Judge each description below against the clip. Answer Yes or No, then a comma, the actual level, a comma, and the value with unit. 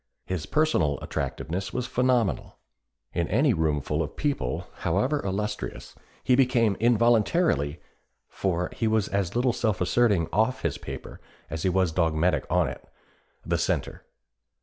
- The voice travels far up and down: Yes, wide, 6.4 semitones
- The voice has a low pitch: Yes, low, 100 Hz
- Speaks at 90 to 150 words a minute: Yes, slow, 135 wpm